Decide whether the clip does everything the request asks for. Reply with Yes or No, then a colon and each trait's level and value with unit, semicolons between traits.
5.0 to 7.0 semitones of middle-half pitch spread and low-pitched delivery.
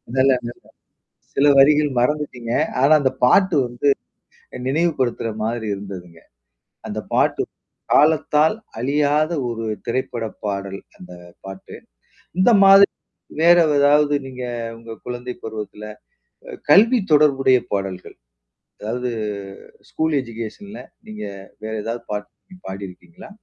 Yes: wide, 5.4 semitones; low, 130 Hz